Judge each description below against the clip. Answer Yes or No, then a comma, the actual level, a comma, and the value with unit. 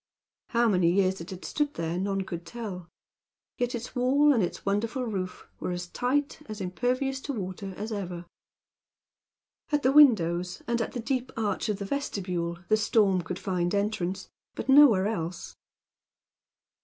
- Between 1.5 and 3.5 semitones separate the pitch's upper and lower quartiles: No, average, 5.2 semitones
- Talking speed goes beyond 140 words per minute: Yes, average, 165 wpm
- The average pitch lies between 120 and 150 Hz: No, high, 205 Hz